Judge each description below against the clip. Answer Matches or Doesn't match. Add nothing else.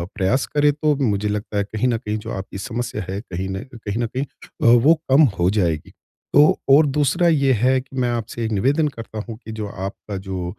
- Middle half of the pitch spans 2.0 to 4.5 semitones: Doesn't match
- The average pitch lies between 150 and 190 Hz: Doesn't match